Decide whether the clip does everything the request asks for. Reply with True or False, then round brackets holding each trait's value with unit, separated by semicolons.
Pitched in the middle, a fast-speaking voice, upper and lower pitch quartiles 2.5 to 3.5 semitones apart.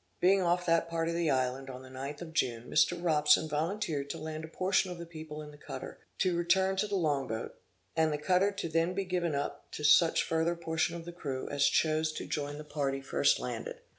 True (160 Hz; 230 wpm; 2.8 semitones)